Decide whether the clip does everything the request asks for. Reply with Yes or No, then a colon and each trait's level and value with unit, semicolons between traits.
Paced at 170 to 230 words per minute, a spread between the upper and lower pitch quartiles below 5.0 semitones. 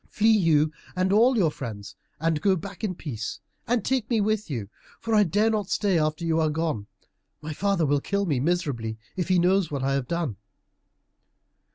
No: average, 195 wpm; wide, 5.6 semitones